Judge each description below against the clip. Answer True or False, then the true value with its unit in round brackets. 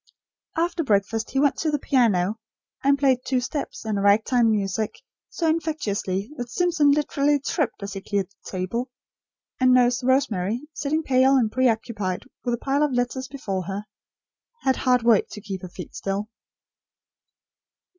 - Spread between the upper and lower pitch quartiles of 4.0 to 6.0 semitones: True (5.4 semitones)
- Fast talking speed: False (160 wpm)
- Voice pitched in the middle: False (245 Hz)